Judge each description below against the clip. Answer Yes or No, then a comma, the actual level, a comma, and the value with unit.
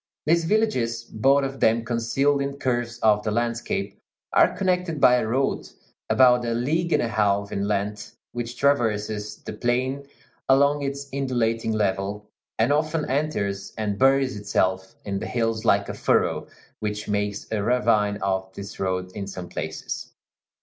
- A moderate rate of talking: Yes, average, 155 wpm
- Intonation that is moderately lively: Yes, average, 4.7 semitones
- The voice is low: Yes, low, 115 Hz